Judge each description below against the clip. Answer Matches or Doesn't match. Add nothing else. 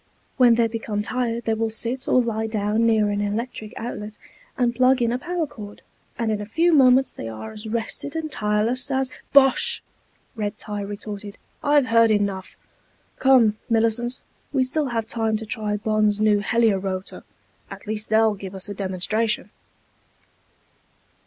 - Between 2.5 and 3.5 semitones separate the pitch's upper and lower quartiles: Matches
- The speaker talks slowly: Doesn't match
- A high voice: Matches